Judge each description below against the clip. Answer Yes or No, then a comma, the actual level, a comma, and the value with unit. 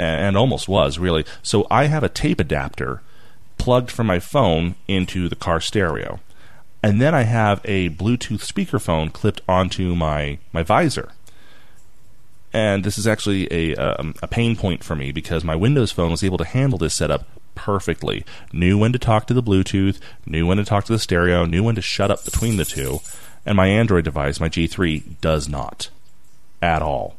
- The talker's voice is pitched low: Yes, very low, 95 Hz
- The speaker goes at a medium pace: Yes, average, 185 wpm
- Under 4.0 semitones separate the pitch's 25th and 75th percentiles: No, average, 4.7 semitones